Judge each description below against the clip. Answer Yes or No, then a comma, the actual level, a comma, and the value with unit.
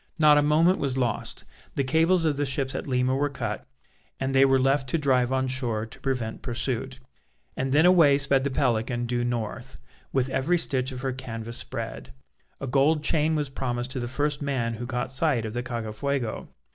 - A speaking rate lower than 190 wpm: No, average, 195 wpm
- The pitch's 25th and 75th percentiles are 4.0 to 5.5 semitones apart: No, average, 2.8 semitones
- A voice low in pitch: Yes, low, 130 Hz